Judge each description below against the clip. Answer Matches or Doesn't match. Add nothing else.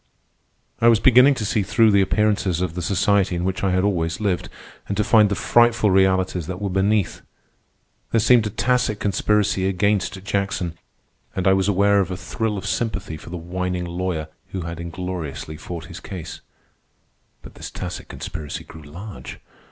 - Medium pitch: Doesn't match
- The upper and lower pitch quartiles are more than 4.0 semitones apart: Doesn't match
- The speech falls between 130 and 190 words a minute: Matches